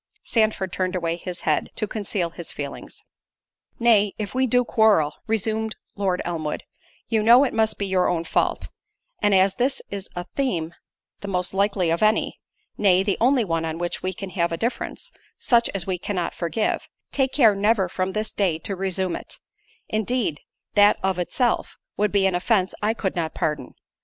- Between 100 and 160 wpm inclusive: No, average, 180 wpm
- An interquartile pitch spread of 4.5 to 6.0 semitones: No, average, 3.6 semitones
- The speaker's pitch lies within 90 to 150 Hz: No, high, 195 Hz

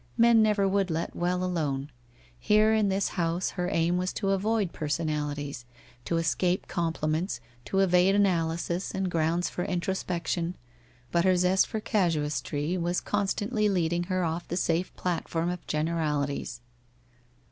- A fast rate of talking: No, average, 145 wpm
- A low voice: No, medium, 175 Hz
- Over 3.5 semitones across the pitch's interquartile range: No, average, 2.7 semitones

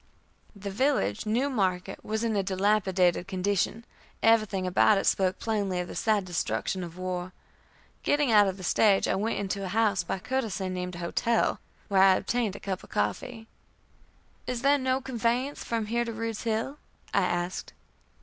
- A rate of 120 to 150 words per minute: No, average, 175 wpm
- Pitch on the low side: No, high, 205 Hz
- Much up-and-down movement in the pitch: No, average, 3.5 semitones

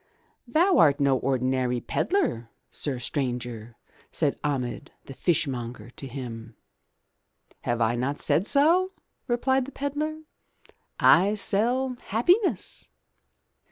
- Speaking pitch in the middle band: Yes, medium, 145 Hz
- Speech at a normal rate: No, slow, 105 wpm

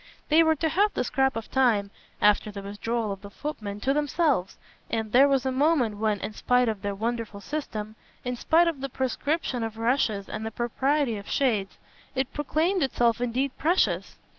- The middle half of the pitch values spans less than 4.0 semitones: No, average, 4.8 semitones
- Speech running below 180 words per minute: No, average, 190 wpm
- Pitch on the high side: Yes, high, 245 Hz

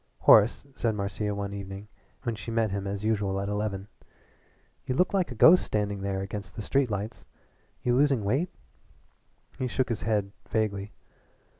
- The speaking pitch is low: Yes, low, 105 Hz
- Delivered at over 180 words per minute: No, average, 165 wpm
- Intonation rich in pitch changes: No, average, 2.8 semitones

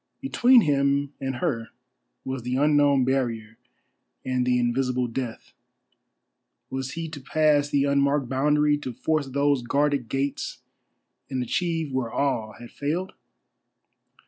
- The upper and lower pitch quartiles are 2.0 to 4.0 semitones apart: Yes, narrow, 2.6 semitones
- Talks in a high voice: No, medium, 140 Hz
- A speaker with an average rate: No, slow, 125 wpm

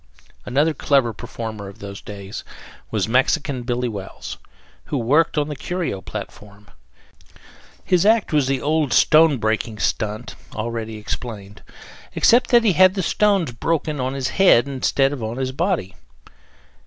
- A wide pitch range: Yes, wide, 6.3 semitones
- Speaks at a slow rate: No, average, 145 wpm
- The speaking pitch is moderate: No, low, 130 Hz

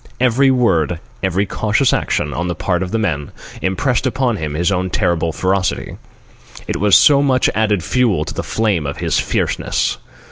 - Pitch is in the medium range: No, low, 100 Hz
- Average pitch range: No, wide, 5.7 semitones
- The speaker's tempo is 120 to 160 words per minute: No, average, 175 wpm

